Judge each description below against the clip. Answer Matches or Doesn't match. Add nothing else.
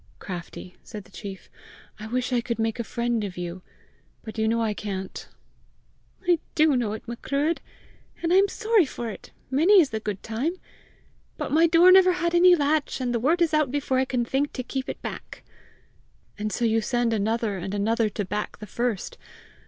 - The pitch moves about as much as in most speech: Doesn't match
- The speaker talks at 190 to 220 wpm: Matches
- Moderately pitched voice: Doesn't match